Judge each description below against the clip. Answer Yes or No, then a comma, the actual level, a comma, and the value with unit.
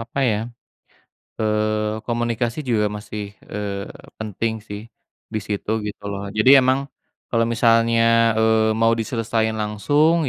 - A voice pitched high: No, low, 110 Hz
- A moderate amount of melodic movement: No, narrow, 1.5 semitones